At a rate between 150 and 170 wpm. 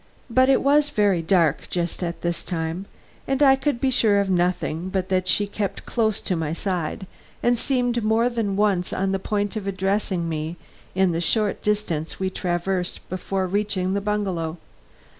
No: average, 180 wpm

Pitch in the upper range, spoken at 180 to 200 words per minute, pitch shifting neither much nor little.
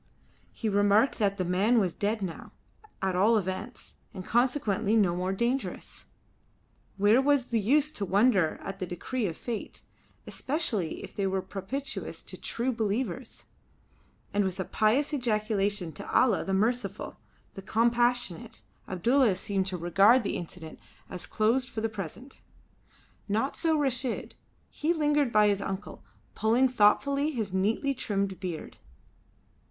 No: high, 215 Hz; average, 145 wpm; average, 4.5 semitones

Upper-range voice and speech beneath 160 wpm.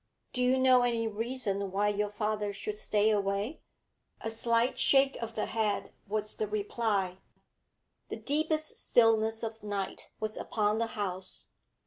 Yes: high, 215 Hz; average, 145 wpm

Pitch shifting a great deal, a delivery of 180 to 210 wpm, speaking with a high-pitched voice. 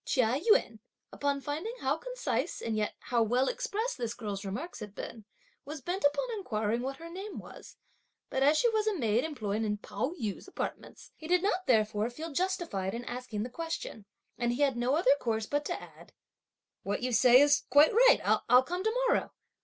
Yes: wide, 7.7 semitones; average, 195 wpm; very high, 270 Hz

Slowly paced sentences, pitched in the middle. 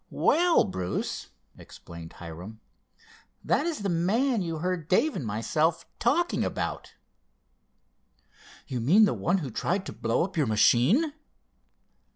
Yes: slow, 130 wpm; medium, 170 Hz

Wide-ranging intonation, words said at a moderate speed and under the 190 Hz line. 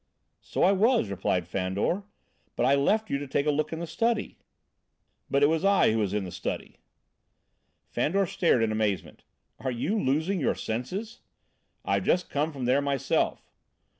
Yes: wide, 8.7 semitones; average, 170 wpm; medium, 140 Hz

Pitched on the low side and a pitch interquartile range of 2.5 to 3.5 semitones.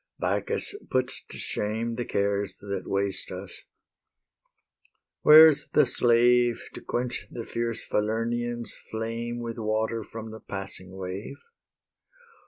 Yes: low, 115 Hz; average, 2.8 semitones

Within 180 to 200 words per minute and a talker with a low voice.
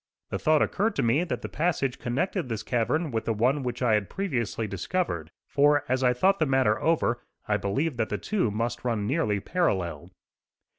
Yes: average, 195 wpm; low, 125 Hz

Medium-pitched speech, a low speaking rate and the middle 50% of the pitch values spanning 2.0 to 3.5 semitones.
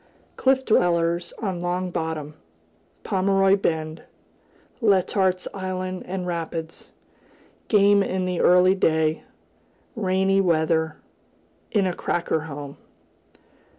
Yes: medium, 180 Hz; slow, 95 wpm; average, 2.8 semitones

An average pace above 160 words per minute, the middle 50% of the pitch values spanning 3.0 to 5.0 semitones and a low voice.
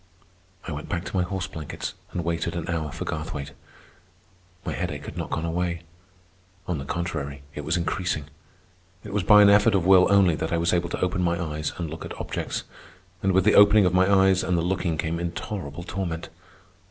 No: fast, 205 wpm; narrow, 2.6 semitones; very low, 85 Hz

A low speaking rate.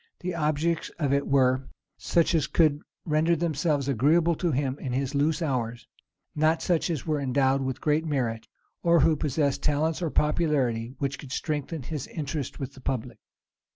No: average, 170 wpm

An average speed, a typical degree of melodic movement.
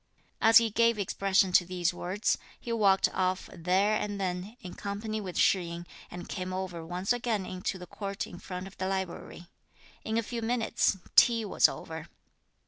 Yes: average, 180 wpm; average, 3.0 semitones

